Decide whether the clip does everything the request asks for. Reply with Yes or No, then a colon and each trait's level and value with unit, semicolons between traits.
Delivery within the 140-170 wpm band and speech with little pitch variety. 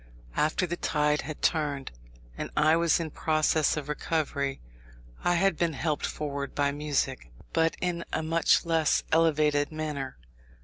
Yes: average, 145 wpm; narrow, 2.1 semitones